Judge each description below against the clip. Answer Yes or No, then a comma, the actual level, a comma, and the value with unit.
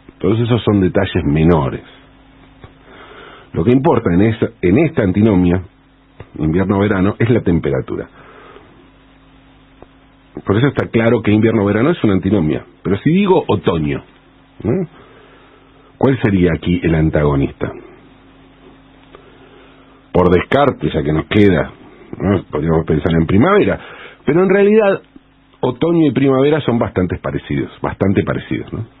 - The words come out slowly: Yes, slow, 120 wpm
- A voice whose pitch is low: Yes, low, 110 Hz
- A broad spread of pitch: Yes, wide, 6.9 semitones